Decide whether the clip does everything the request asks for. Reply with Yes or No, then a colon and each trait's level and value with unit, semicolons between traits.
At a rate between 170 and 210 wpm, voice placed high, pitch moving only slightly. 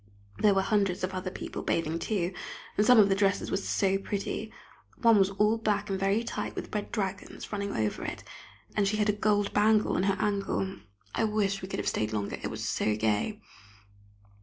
Yes: fast, 205 wpm; high, 200 Hz; narrow, 1.7 semitones